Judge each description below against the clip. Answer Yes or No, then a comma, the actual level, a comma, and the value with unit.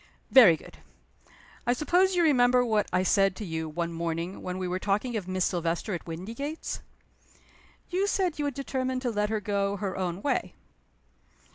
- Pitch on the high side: Yes, high, 205 Hz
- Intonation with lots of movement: Yes, wide, 6.1 semitones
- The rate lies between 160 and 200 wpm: Yes, average, 175 wpm